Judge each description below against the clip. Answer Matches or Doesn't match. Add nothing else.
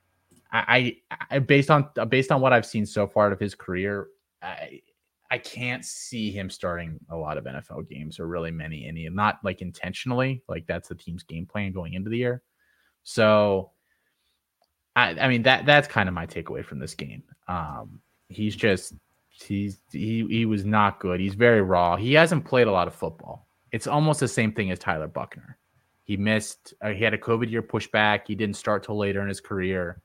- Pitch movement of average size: Matches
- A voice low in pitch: Matches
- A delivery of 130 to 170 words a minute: Doesn't match